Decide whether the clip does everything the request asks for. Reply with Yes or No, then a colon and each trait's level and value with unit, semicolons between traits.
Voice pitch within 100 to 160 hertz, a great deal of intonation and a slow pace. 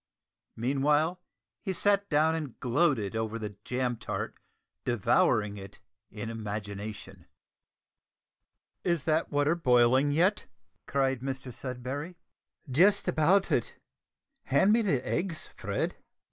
Yes: low, 135 Hz; wide, 6.0 semitones; slow, 110 wpm